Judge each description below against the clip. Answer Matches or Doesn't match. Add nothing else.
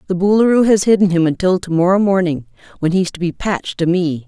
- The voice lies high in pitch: Doesn't match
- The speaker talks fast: Matches